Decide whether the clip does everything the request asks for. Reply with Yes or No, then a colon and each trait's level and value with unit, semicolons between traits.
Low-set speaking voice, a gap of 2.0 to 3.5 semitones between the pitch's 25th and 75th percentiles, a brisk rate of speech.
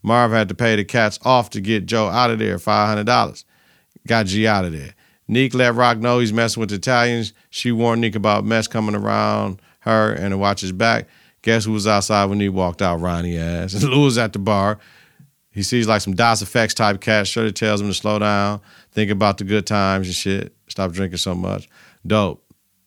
Yes: low, 105 Hz; narrow, 2.6 semitones; fast, 210 wpm